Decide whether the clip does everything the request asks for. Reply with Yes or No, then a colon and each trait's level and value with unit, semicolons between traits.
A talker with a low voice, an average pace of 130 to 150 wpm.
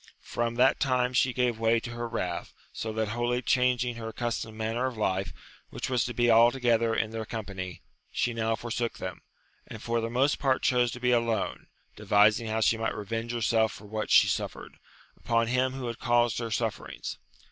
No: low, 115 Hz; average, 190 wpm